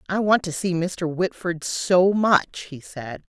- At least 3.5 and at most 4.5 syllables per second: Yes, 3.6 syllables/s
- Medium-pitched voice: Yes, medium, 175 Hz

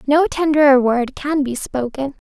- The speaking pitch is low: No, very high, 275 Hz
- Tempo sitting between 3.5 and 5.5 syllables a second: Yes, 4.4 syllables/s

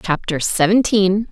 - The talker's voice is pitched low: No, high, 195 Hz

